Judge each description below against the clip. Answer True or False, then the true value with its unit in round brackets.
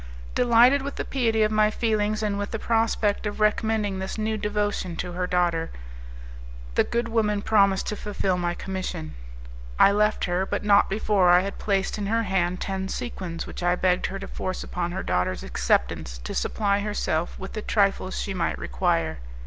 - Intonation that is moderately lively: True (3.0 semitones)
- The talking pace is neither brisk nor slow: True (185 wpm)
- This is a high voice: True (200 Hz)